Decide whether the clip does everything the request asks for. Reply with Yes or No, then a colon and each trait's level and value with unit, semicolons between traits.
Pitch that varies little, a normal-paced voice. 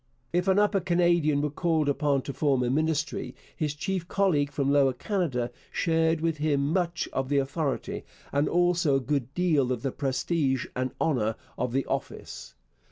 No: average, 3.9 semitones; average, 170 wpm